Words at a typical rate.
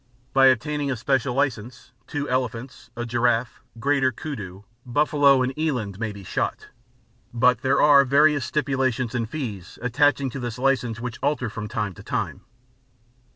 Yes: average, 155 wpm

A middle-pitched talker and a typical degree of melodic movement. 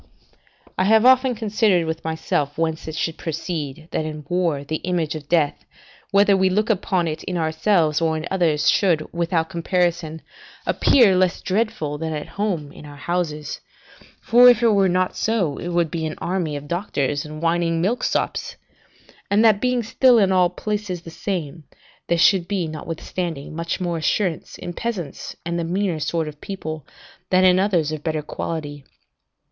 Yes: medium, 170 Hz; average, 3.4 semitones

